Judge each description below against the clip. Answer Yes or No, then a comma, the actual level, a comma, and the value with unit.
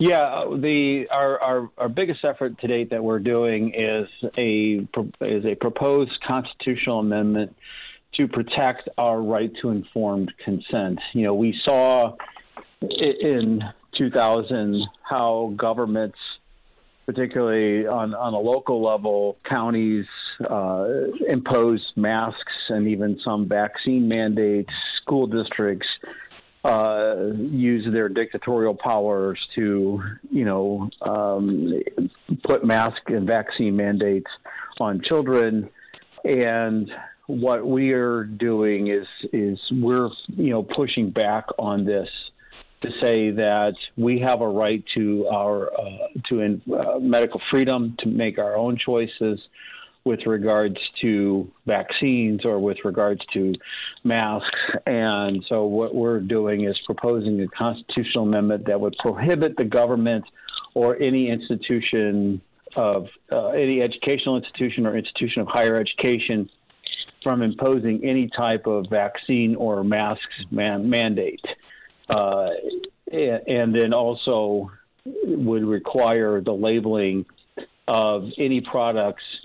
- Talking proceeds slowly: Yes, slow, 120 wpm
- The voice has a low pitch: Yes, low, 110 Hz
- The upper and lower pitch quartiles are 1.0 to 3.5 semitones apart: Yes, narrow, 2.6 semitones